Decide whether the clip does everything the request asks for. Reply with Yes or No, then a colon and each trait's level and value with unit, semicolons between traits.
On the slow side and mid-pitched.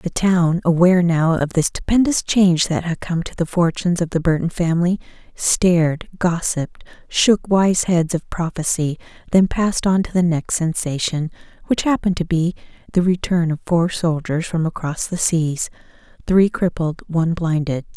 No: average, 160 wpm; medium, 170 Hz